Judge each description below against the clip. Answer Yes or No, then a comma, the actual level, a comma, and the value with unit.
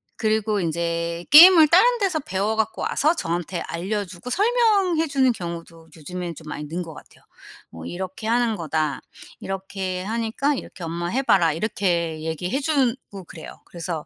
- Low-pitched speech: No, high, 190 Hz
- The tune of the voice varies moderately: No, wide, 7.5 semitones